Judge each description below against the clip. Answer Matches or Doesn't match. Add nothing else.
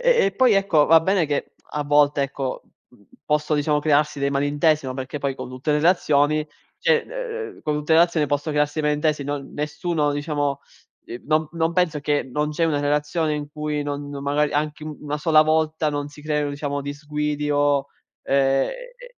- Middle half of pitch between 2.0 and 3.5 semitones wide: Doesn't match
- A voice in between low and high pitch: Matches